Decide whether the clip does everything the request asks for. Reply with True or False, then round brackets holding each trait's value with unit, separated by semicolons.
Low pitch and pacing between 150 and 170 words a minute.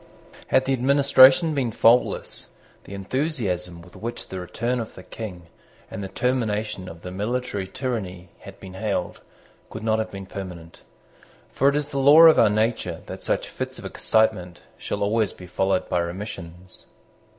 True (105 Hz; 165 wpm)